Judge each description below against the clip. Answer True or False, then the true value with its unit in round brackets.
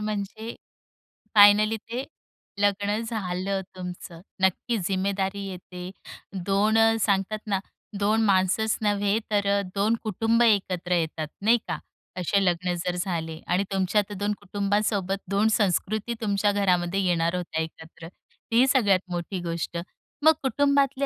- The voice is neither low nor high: False (200 Hz)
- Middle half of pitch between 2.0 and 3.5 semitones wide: True (2.9 semitones)